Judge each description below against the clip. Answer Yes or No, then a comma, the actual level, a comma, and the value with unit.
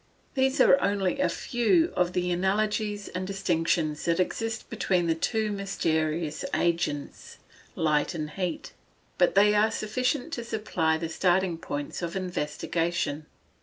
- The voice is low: No, medium, 180 Hz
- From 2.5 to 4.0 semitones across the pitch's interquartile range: No, average, 4.4 semitones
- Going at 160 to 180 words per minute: No, slow, 135 wpm